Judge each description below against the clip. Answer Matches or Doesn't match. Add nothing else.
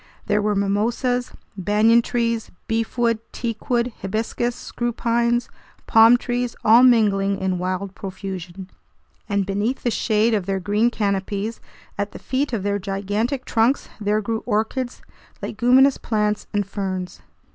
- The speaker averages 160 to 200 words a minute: Doesn't match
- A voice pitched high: Matches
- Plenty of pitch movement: Doesn't match